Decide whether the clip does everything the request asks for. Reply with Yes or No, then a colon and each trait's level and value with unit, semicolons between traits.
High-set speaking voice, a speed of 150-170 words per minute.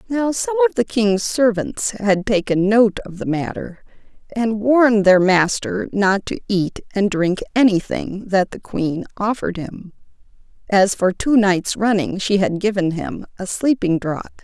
Yes: high, 205 Hz; average, 160 wpm